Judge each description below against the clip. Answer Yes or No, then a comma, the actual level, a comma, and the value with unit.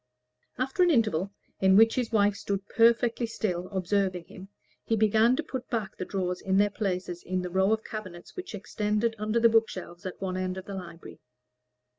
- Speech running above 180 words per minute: Yes, average, 190 wpm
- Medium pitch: No, high, 205 Hz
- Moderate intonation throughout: Yes, average, 3.4 semitones